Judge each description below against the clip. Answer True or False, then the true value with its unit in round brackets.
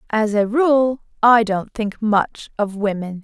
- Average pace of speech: True (165 wpm)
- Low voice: False (220 Hz)